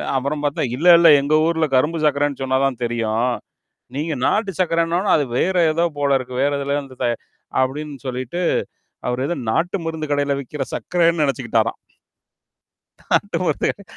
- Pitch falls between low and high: Yes, medium, 145 Hz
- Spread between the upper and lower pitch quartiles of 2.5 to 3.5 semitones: No, average, 4.0 semitones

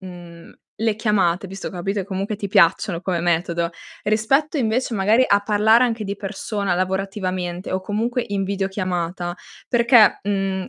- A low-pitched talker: No, high, 195 Hz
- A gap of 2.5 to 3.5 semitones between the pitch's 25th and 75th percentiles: Yes, average, 2.8 semitones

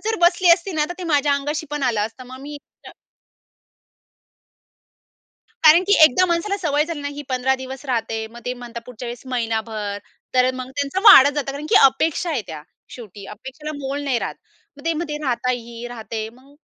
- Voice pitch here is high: Yes, very high, 265 Hz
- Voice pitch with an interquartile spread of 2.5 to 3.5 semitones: No, average, 4.0 semitones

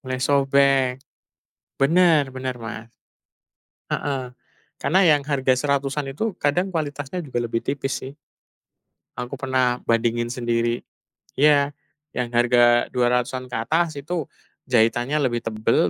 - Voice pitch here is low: Yes, low, 130 Hz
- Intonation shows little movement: No, average, 3.1 semitones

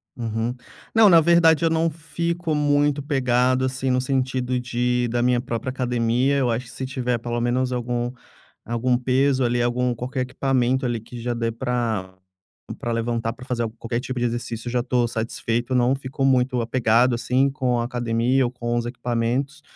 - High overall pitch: No, low, 125 Hz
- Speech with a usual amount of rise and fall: No, narrow, 1.7 semitones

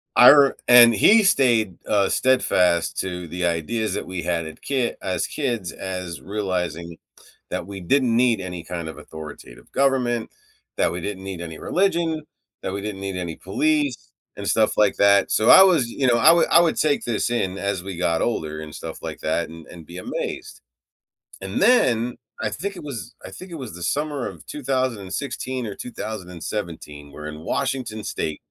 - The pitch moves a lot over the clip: Yes, wide, 6.8 semitones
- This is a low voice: Yes, low, 105 Hz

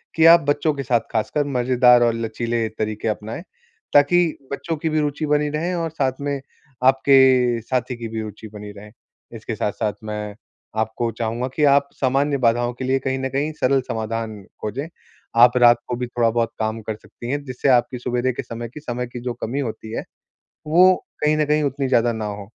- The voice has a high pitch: No, low, 125 Hz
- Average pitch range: Yes, average, 3.8 semitones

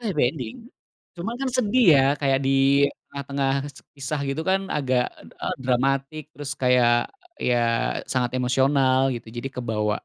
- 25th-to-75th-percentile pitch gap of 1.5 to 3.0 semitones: Yes, narrow, 2.6 semitones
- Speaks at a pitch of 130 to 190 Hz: Yes, low, 135 Hz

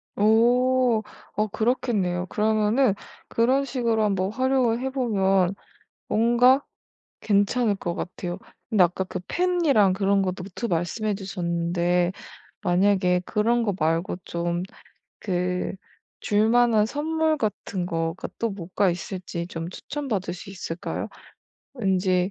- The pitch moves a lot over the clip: No, average, 4.7 semitones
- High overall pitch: Yes, high, 205 Hz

